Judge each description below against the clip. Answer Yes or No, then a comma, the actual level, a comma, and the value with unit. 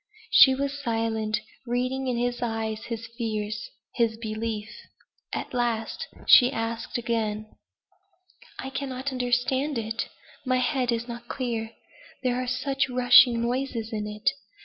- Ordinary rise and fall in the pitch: No, narrow, 2.2 semitones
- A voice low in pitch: No, high, 240 Hz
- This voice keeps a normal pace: No, slow, 130 wpm